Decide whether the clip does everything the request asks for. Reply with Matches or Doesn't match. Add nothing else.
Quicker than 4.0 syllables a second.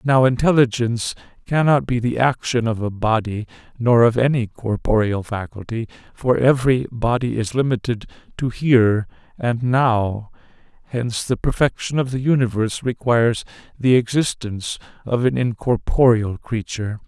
Matches